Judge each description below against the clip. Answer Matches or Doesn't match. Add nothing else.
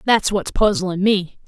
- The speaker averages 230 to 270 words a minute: Doesn't match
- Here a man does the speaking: Doesn't match